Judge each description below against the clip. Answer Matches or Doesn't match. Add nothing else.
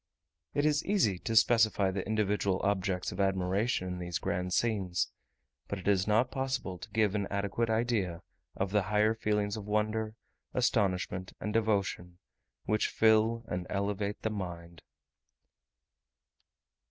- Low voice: Matches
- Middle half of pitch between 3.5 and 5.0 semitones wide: Doesn't match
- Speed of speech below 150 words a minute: Matches